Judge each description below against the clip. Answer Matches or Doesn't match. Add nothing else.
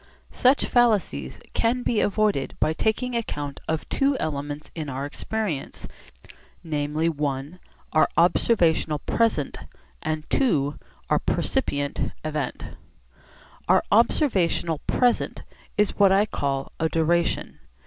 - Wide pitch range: Matches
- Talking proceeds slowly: Matches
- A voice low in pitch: Doesn't match